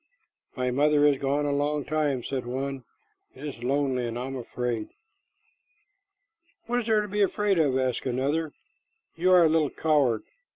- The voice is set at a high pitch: No, medium, 140 Hz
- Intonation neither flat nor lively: Yes, average, 3.4 semitones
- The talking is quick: No, average, 170 wpm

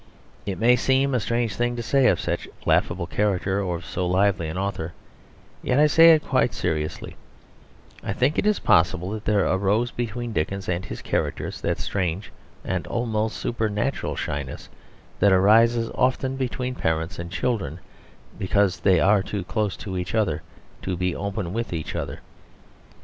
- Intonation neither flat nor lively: Yes, average, 4.6 semitones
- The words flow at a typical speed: Yes, average, 165 wpm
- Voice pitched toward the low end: Yes, low, 100 Hz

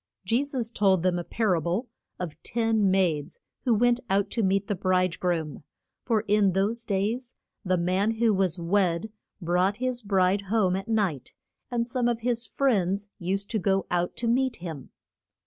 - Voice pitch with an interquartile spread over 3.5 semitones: Yes, average, 3.9 semitones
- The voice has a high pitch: Yes, high, 200 Hz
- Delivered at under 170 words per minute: No, average, 180 wpm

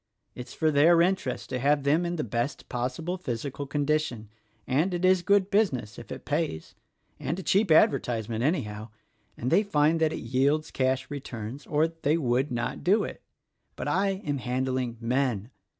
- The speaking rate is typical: Yes, average, 180 wpm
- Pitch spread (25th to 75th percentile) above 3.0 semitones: Yes, average, 5.0 semitones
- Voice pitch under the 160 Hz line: Yes, medium, 140 Hz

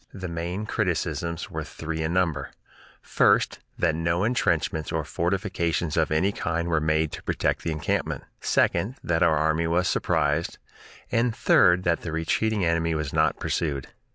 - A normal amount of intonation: No, narrow, 2.2 semitones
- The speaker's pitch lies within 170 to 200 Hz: No, very low, 85 Hz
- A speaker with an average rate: Yes, average, 155 wpm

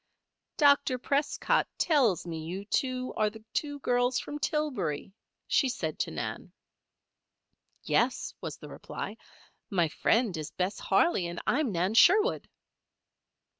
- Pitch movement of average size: No, wide, 7.5 semitones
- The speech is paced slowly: Yes, slow, 130 wpm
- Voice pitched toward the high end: Yes, high, 245 Hz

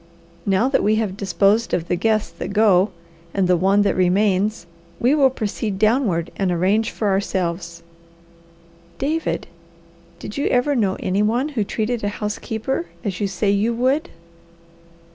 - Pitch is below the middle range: No, high, 210 Hz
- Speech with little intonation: No, average, 3.4 semitones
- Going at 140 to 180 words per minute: Yes, average, 155 wpm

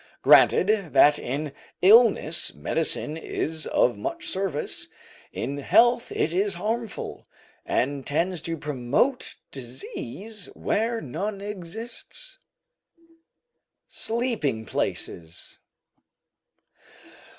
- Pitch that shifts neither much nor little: No, wide, 7.3 semitones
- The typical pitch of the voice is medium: Yes, medium, 175 Hz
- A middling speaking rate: No, slow, 85 wpm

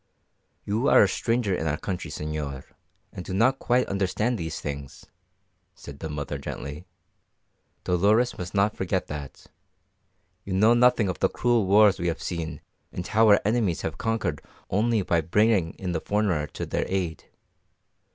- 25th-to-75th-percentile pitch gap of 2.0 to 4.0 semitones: No, average, 5.1 semitones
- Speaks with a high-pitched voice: No, very low, 95 Hz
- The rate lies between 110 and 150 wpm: No, average, 160 wpm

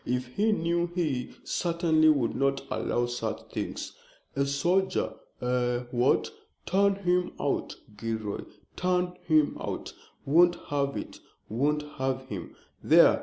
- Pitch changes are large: Yes, wide, 6.0 semitones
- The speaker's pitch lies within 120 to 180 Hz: Yes, medium, 140 Hz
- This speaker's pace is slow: Yes, slow, 125 wpm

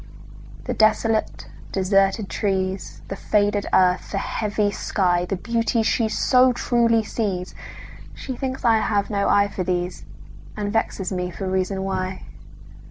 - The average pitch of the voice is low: No, high, 200 Hz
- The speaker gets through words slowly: Yes, slow, 120 wpm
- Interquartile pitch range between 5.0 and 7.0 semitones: No, average, 2.9 semitones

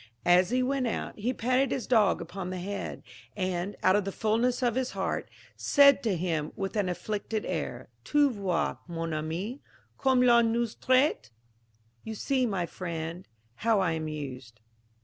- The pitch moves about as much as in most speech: No, wide, 5.9 semitones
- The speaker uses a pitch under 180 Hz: No, high, 205 Hz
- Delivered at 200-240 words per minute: No, average, 170 wpm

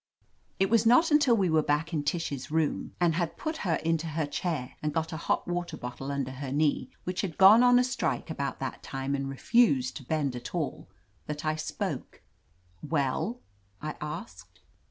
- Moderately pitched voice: Yes, medium, 155 Hz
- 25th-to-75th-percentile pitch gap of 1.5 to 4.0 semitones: No, average, 4.4 semitones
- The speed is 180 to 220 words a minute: Yes, average, 190 wpm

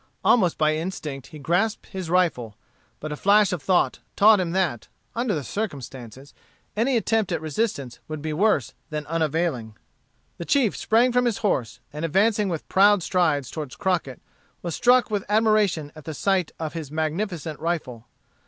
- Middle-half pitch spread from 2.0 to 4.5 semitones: No, wide, 5.5 semitones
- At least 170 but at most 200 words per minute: No, average, 160 wpm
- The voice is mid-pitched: Yes, medium, 170 Hz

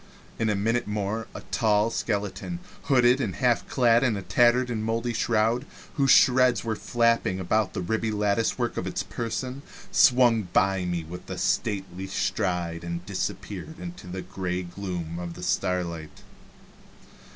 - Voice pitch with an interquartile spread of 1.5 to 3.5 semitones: No, average, 4.4 semitones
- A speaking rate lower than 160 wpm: Yes, average, 150 wpm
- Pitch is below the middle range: Yes, low, 105 Hz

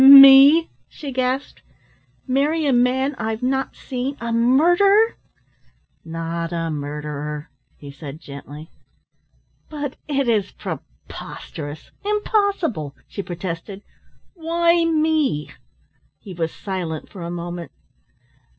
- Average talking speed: No, slow, 105 wpm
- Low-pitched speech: No, high, 235 Hz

